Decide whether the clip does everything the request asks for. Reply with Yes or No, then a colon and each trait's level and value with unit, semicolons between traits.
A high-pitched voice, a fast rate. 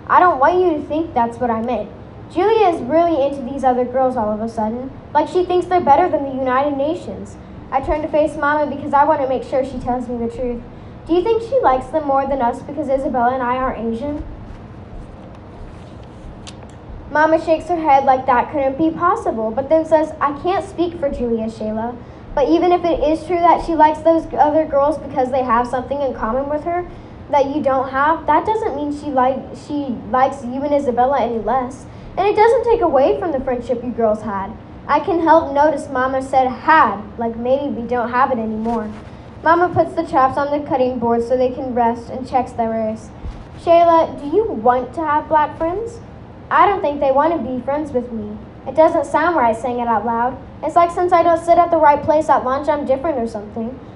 Yes: very high, 280 Hz; fast, 220 wpm